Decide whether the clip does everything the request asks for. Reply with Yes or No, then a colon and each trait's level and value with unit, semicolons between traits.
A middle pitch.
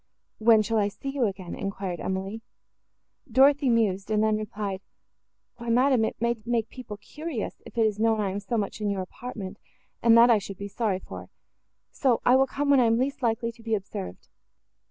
No: high, 225 Hz